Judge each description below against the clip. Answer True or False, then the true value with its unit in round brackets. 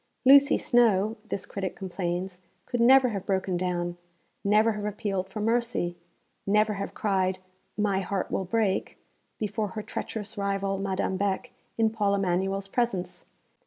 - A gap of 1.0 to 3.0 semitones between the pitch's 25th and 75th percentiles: True (2.4 semitones)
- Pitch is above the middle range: True (200 Hz)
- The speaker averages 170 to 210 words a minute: False (145 wpm)